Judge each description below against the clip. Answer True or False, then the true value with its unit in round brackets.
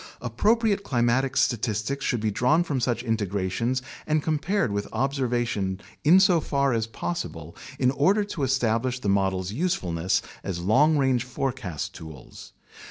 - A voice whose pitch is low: True (125 Hz)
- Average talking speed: False (130 wpm)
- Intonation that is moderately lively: False (5.8 semitones)